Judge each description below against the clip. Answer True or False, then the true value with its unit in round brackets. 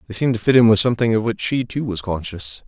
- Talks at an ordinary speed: False (290 wpm)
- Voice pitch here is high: False (110 Hz)